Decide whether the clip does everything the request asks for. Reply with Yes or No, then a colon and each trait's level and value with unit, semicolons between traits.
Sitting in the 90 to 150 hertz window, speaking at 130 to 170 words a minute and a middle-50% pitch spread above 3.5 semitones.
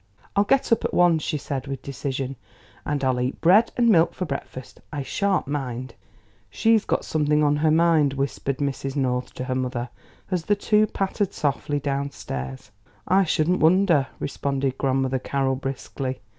Yes: medium, 140 Hz; average, 165 wpm; average, 4.2 semitones